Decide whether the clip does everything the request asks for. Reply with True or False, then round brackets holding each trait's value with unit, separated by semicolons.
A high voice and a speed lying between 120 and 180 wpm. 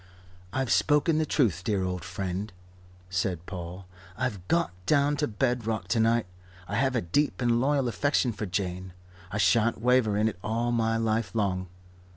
False (110 Hz; 175 wpm)